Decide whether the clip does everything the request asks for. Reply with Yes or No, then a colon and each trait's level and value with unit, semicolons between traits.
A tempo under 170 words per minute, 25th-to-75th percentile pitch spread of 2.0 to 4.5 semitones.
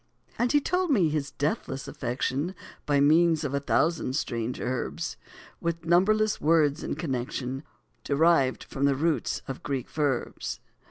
Yes: average, 145 wpm; average, 4.0 semitones